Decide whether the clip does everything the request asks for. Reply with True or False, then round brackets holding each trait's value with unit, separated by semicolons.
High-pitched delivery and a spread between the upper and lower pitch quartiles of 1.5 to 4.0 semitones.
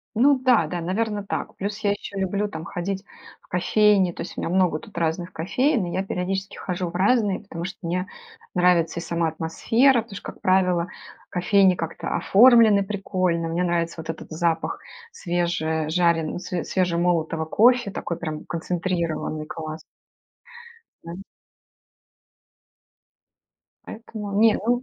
False (180 Hz; 3.3 semitones)